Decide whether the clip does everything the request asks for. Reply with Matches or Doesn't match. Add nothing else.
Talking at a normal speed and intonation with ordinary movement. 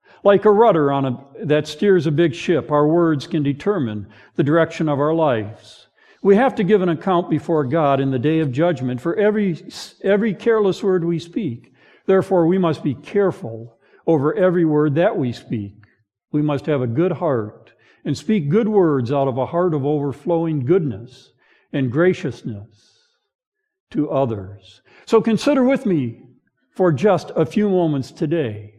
Doesn't match